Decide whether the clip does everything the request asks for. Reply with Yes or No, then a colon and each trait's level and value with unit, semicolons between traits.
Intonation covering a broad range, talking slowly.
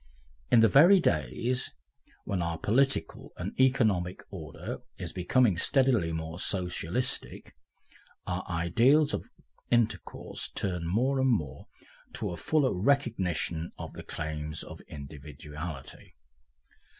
Yes: wide, 7.8 semitones; slow, 115 wpm